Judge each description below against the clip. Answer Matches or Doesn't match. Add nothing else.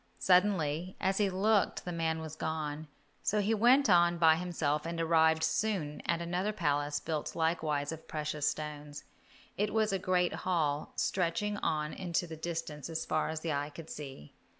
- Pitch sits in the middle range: Matches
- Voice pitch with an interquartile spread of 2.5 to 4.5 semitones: Matches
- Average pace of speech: Matches